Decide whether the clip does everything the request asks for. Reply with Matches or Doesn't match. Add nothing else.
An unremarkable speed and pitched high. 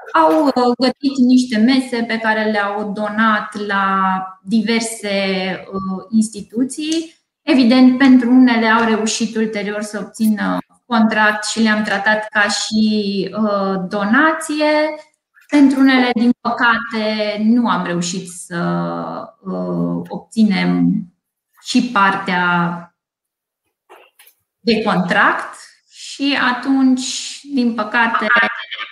Doesn't match